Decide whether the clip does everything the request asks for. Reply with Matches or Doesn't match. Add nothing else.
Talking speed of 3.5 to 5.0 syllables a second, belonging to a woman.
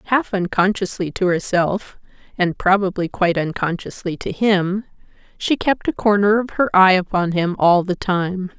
Matches